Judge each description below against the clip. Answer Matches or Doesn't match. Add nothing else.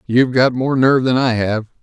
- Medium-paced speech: Doesn't match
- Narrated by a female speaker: Doesn't match